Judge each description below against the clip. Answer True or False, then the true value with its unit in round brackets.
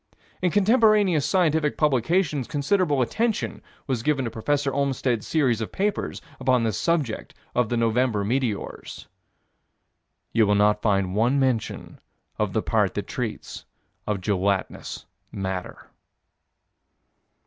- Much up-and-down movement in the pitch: True (5.9 semitones)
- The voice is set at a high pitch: False (130 Hz)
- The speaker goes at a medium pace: False (120 wpm)